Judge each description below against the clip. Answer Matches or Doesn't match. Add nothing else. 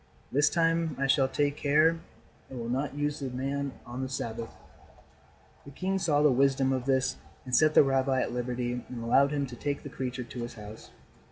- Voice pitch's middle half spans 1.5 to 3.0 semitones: Matches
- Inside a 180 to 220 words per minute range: Matches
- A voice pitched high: Doesn't match